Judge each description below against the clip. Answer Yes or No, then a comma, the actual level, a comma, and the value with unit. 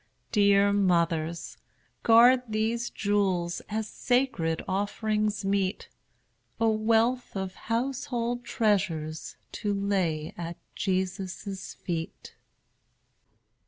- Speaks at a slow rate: Yes, slow, 85 wpm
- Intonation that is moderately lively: Yes, average, 3.5 semitones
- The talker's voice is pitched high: Yes, high, 200 Hz